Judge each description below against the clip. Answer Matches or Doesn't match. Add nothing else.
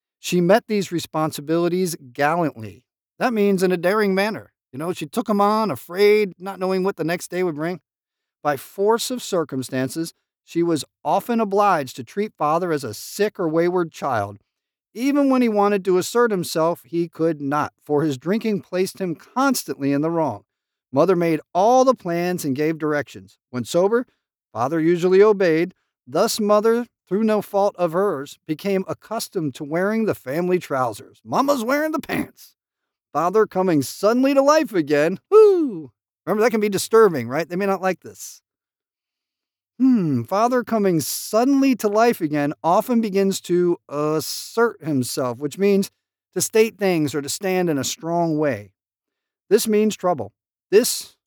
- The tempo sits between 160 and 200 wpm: Matches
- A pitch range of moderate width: Doesn't match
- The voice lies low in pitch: Doesn't match